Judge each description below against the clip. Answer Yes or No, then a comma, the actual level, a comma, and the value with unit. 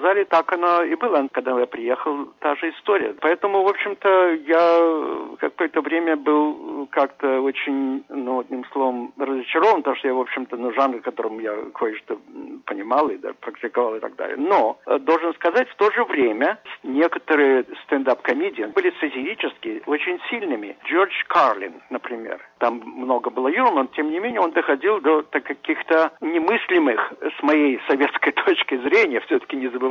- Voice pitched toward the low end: No, medium, 160 Hz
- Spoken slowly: No, average, 155 wpm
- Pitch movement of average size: No, wide, 6.9 semitones